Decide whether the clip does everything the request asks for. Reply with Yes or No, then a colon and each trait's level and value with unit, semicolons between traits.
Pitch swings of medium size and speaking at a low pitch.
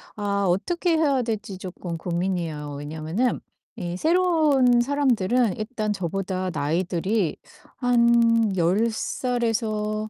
No: average, 5.0 semitones; high, 215 Hz